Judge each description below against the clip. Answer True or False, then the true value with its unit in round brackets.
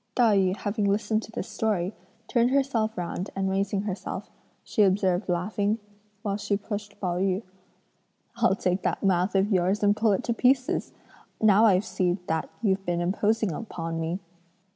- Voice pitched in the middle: False (200 Hz)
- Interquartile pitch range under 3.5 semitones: True (2.8 semitones)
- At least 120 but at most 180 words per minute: True (170 wpm)